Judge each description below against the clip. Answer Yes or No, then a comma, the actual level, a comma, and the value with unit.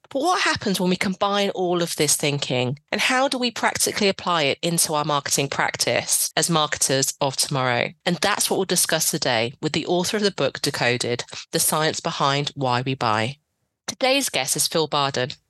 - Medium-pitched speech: Yes, medium, 155 Hz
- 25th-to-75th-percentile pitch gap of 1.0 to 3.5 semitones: No, average, 5.3 semitones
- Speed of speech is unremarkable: Yes, average, 190 wpm